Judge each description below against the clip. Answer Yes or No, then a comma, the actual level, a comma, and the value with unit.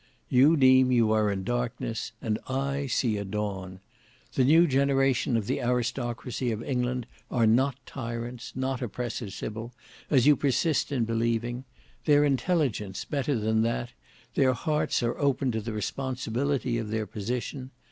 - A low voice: Yes, low, 125 Hz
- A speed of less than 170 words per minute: Yes, average, 150 wpm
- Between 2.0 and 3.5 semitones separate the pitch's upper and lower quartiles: Yes, average, 3.1 semitones